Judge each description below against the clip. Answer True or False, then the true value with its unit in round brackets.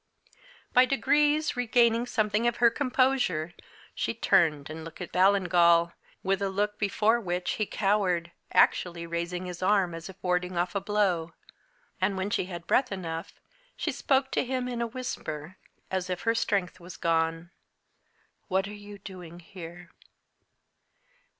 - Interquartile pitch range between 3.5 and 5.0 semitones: True (4.6 semitones)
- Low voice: False (190 Hz)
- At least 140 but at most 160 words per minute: True (150 wpm)